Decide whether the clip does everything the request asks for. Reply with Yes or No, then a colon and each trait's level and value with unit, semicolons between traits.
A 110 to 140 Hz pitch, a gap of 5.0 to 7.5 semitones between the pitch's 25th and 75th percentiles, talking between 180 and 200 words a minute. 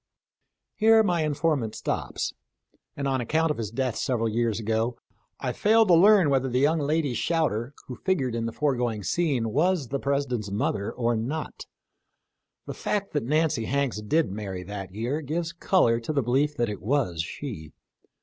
No: low, 135 Hz; wide, 5.6 semitones; average, 170 wpm